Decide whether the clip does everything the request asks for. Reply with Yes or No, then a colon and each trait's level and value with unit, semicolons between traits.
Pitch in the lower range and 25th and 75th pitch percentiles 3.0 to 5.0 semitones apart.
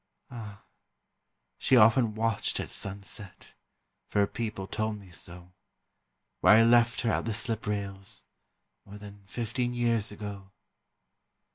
No: low, 105 Hz; narrow, 2.4 semitones